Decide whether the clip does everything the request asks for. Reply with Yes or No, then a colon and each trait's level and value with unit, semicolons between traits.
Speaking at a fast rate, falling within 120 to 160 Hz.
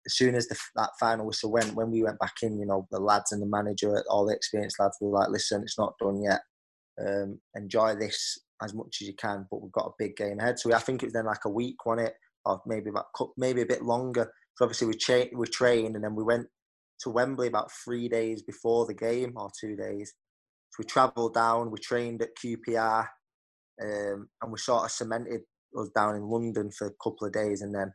No: fast, 245 wpm; low, 110 Hz